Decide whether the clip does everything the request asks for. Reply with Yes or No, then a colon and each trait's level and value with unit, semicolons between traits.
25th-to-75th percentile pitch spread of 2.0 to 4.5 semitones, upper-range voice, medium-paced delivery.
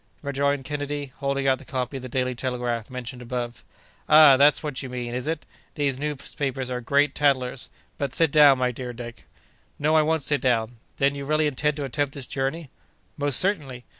No: narrow, 2.5 semitones; low, 135 Hz; average, 190 wpm